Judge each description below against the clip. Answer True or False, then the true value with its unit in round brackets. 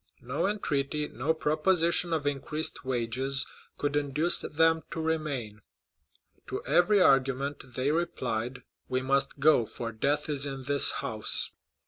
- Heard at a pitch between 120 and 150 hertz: True (140 Hz)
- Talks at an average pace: False (130 wpm)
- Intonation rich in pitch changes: False (3.4 semitones)